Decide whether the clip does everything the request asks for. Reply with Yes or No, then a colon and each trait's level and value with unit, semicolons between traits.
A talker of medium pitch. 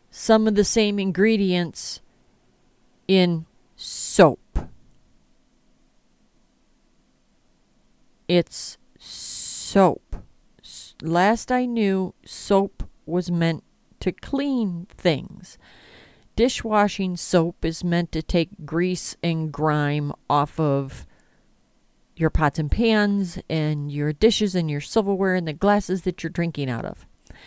Yes: medium, 175 Hz